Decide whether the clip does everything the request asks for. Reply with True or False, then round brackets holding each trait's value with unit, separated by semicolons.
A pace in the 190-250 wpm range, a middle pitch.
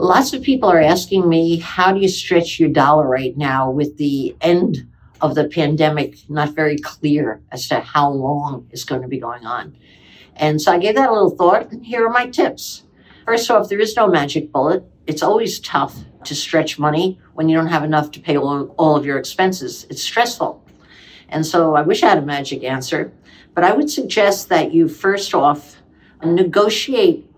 True (200 wpm; 155 Hz)